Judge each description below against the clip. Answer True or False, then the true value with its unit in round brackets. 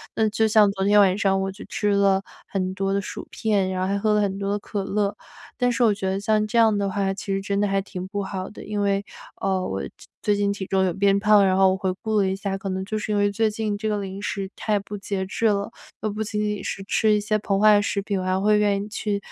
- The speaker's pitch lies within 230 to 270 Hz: False (200 Hz)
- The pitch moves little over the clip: True (1.5 semitones)